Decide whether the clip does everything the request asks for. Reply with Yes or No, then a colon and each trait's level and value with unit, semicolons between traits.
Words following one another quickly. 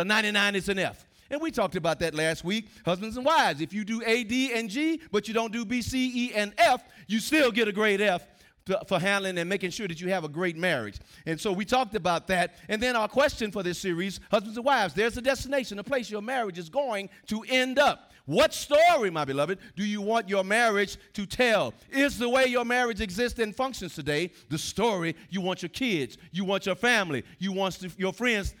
Yes: fast, 230 wpm